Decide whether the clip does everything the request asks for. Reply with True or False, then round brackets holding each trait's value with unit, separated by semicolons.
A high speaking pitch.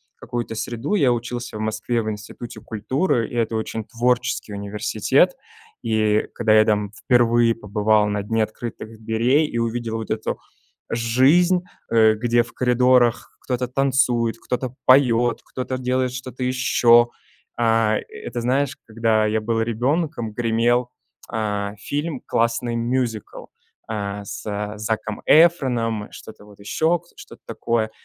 False (115 Hz)